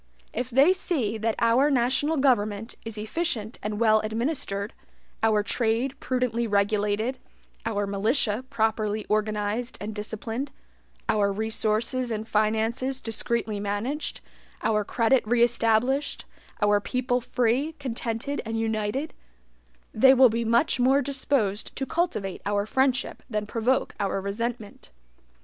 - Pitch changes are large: No, average, 3.4 semitones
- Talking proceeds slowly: Yes, slow, 125 wpm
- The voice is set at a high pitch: Yes, high, 225 Hz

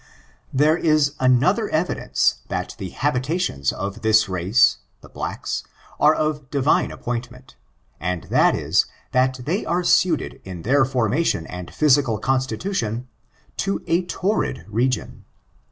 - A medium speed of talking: No, slow, 125 wpm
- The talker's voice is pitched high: No, low, 130 Hz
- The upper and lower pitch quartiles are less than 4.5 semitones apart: No, wide, 5.6 semitones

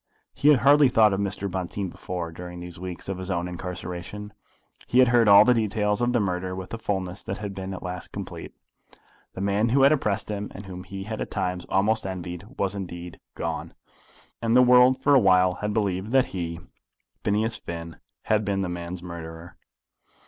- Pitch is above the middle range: No, very low, 95 Hz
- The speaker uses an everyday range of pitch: Yes, average, 3.3 semitones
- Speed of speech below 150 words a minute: No, average, 195 wpm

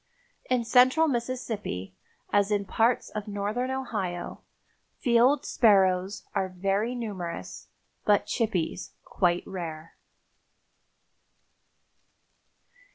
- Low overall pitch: No, high, 205 Hz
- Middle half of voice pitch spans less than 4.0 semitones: No, average, 4.6 semitones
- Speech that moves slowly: Yes, slow, 85 wpm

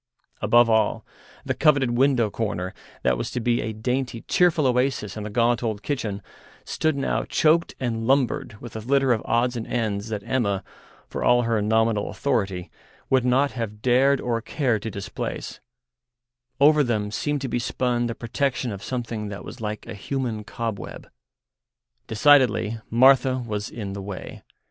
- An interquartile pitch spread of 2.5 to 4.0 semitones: Yes, average, 3.4 semitones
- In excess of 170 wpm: No, average, 165 wpm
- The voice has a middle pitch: No, low, 115 Hz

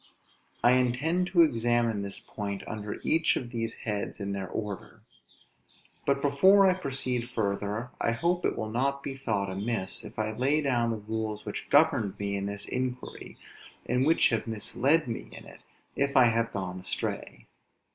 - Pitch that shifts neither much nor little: Yes, average, 4.6 semitones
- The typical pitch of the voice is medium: No, low, 115 Hz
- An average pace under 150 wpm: No, average, 170 wpm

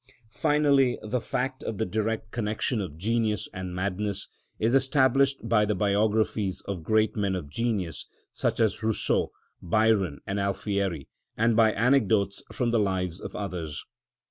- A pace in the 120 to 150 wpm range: Yes, average, 145 wpm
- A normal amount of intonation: Yes, average, 3.0 semitones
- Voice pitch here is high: No, low, 105 Hz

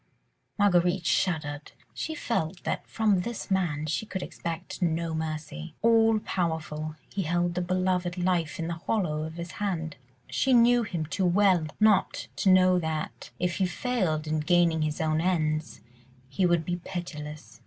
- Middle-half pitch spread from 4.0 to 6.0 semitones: No, average, 3.2 semitones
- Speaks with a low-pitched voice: No, medium, 175 Hz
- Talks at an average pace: Yes, average, 160 wpm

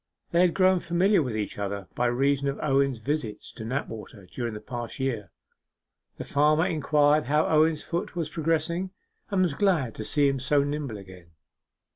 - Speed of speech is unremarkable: Yes, average, 175 wpm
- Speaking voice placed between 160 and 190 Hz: No, medium, 140 Hz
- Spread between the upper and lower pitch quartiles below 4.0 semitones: No, average, 5.3 semitones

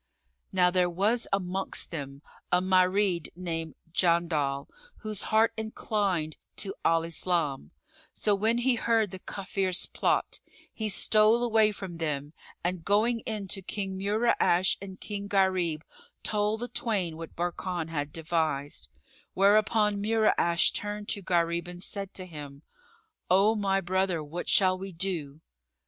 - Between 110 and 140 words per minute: Yes, slow, 135 wpm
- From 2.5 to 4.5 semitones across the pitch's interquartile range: Yes, average, 3.6 semitones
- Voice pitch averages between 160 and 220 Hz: Yes, medium, 185 Hz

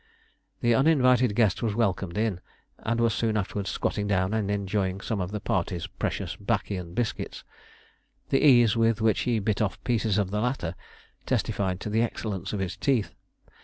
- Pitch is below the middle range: Yes, low, 105 Hz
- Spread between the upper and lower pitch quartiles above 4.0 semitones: No, average, 3.1 semitones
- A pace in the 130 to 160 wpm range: No, average, 175 wpm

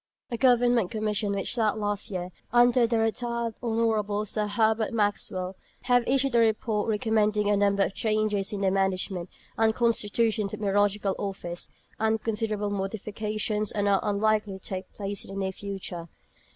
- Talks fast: No, average, 165 wpm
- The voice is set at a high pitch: Yes, high, 210 Hz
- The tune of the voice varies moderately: No, narrow, 2.0 semitones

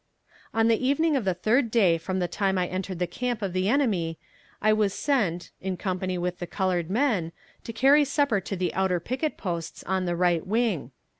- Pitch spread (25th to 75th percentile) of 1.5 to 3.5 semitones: No, average, 4.5 semitones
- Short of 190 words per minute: No, fast, 205 wpm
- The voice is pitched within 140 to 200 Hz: Yes, high, 190 Hz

